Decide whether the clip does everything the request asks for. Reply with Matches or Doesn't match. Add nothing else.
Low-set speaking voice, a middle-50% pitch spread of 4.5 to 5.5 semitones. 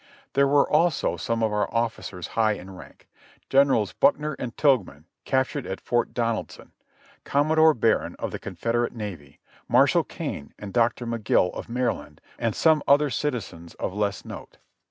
Matches